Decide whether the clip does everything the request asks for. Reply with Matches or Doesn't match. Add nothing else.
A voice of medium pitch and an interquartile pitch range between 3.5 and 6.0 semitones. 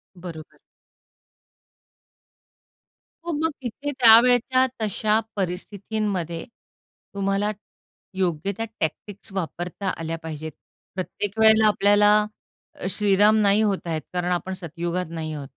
Doesn't match